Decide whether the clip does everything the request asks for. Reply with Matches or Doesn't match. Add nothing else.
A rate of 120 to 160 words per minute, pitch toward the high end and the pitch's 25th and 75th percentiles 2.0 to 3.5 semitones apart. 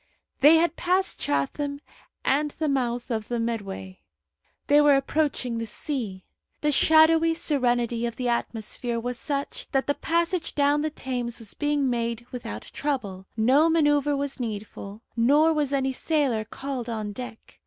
Doesn't match